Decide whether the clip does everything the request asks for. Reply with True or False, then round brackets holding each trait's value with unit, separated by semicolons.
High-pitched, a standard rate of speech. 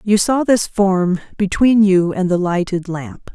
True (195 Hz; 180 wpm)